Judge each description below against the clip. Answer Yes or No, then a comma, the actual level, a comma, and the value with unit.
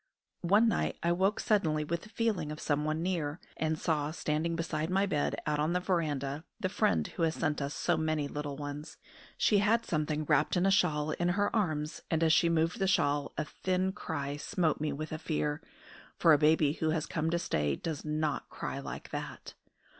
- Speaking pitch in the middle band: Yes, medium, 155 Hz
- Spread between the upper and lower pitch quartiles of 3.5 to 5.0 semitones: No, average, 3.0 semitones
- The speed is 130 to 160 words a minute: No, fast, 205 wpm